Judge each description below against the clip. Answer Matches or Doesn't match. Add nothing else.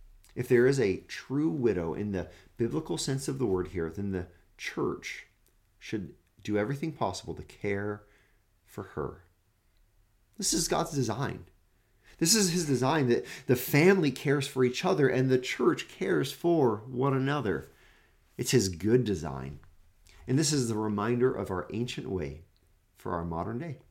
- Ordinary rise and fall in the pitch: Doesn't match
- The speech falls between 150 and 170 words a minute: Matches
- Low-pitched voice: Matches